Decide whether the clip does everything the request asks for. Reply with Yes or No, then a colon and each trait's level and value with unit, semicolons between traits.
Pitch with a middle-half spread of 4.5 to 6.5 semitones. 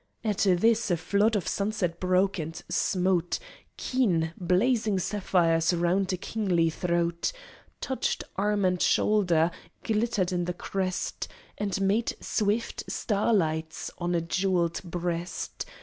No: average, 3.2 semitones